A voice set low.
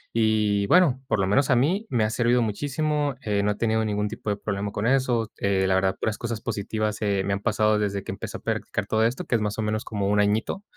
Yes: low, 110 Hz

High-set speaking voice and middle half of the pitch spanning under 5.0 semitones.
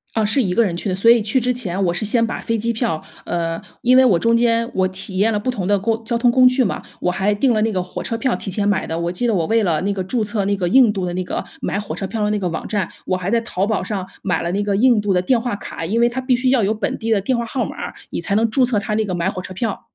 Yes: high, 210 Hz; average, 3.7 semitones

